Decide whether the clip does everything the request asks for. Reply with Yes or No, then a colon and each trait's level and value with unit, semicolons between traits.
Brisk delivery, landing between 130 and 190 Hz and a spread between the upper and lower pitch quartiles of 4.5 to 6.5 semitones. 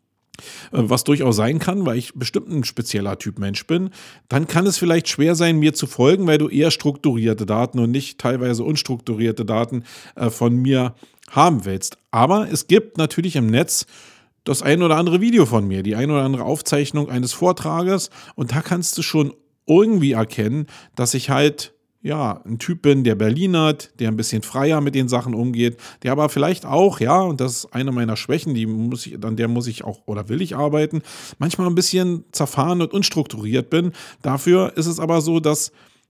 Yes: fast, 195 wpm; medium, 140 Hz; wide, 5.5 semitones